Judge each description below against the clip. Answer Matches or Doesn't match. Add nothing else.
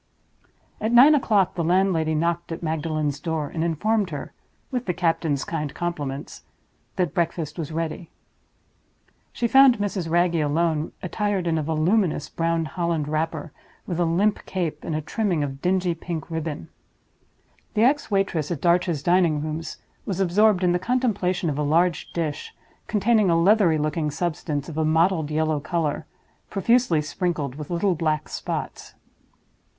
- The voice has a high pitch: Doesn't match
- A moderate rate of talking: Matches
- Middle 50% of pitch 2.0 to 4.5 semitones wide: Matches